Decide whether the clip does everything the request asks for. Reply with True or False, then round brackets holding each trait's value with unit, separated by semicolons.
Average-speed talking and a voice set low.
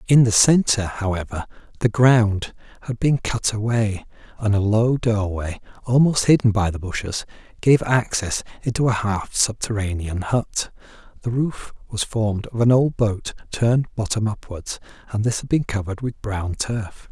True (160 wpm; 110 Hz)